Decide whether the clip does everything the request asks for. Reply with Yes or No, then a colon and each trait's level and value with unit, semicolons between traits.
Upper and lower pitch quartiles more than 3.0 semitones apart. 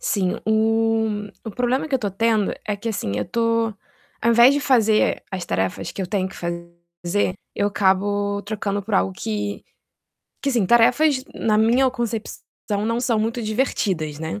Yes: average, 3.4 semitones